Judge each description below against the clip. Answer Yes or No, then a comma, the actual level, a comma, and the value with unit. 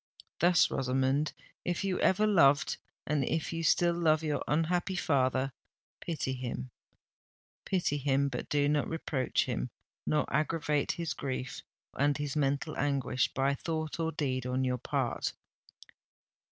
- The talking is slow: Yes, slow, 125 wpm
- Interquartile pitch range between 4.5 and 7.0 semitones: No, average, 3.5 semitones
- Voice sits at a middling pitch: Yes, medium, 145 Hz